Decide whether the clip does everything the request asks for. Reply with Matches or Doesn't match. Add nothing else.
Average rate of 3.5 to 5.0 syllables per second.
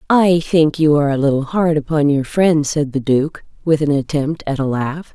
Matches